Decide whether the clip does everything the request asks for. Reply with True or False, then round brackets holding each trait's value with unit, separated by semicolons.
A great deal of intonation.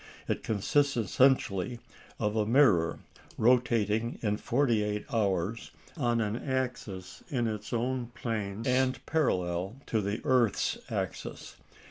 False (3.6 semitones)